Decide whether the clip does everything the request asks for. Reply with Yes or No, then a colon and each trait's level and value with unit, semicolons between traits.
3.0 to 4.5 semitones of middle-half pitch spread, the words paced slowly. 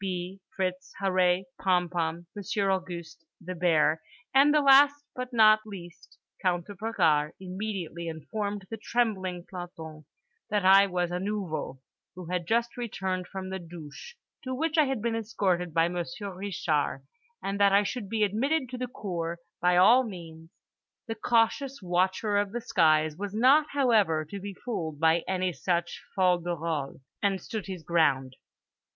No: average, 4.0 semitones; average, 160 wpm